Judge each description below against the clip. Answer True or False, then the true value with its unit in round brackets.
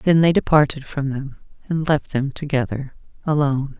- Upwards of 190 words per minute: False (160 wpm)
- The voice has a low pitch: False (145 Hz)